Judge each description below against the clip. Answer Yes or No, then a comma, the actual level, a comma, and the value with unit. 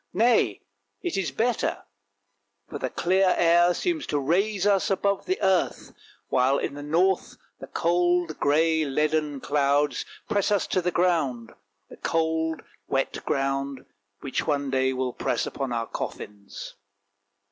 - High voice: No, medium, 160 Hz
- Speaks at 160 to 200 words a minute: No, average, 145 wpm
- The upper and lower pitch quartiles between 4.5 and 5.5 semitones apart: Yes, average, 5.1 semitones